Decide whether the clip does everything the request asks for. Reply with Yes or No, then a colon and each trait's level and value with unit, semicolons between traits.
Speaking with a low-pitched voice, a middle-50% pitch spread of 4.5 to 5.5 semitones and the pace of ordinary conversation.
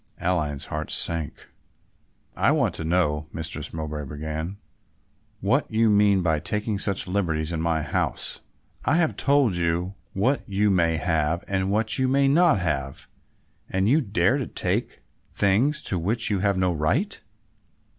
Yes: very low, 95 Hz; average, 5.1 semitones; average, 155 wpm